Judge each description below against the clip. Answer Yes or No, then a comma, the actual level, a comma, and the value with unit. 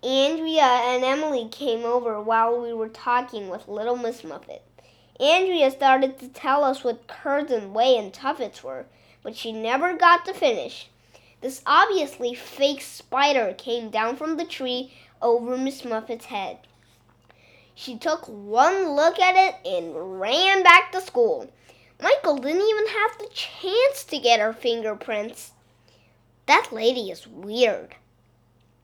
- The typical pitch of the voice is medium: No, very high, 255 Hz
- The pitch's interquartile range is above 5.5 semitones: Yes, wide, 6.0 semitones